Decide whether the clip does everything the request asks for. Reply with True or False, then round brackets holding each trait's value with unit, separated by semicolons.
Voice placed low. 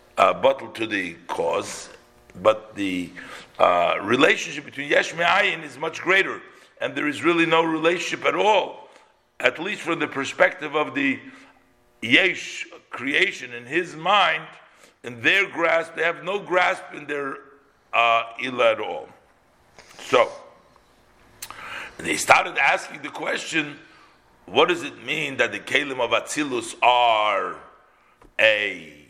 False (165 Hz)